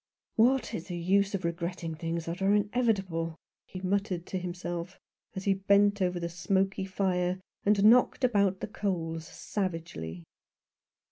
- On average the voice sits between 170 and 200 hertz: Yes, medium, 185 Hz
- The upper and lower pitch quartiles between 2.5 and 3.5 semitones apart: Yes, average, 2.9 semitones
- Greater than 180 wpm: No, average, 150 wpm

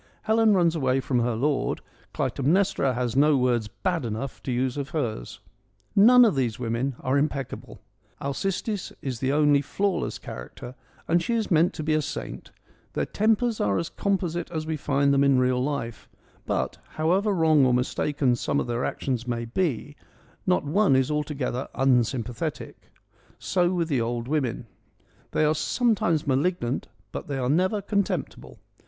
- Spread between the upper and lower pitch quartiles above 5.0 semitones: Yes, wide, 5.4 semitones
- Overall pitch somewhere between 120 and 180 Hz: Yes, medium, 140 Hz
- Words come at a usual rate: Yes, average, 170 wpm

